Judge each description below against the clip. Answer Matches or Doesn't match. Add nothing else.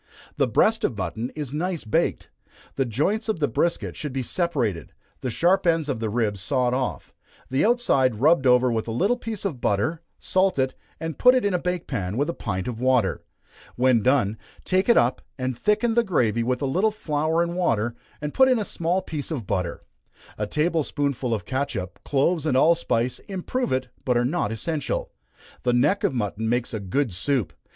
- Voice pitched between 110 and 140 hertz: Matches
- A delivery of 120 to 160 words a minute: Doesn't match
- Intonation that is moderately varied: Doesn't match